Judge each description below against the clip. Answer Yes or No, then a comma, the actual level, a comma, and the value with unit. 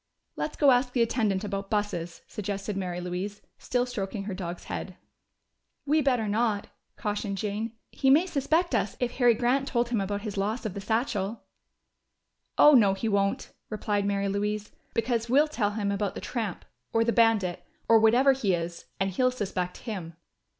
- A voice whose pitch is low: No, high, 210 Hz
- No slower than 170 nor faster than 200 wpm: Yes, average, 175 wpm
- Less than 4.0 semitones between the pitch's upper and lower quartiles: Yes, average, 3.5 semitones